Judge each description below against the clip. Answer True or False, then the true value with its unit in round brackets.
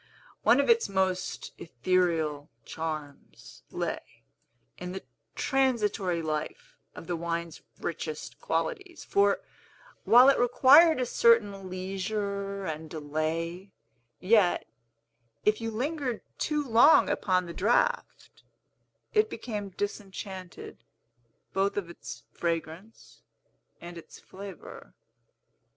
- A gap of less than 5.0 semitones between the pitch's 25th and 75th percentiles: False (5.5 semitones)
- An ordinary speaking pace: False (100 wpm)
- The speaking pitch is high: True (195 Hz)